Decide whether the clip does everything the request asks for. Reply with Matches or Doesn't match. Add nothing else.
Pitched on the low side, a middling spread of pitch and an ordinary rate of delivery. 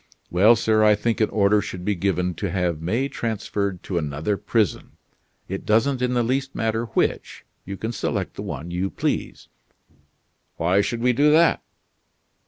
Matches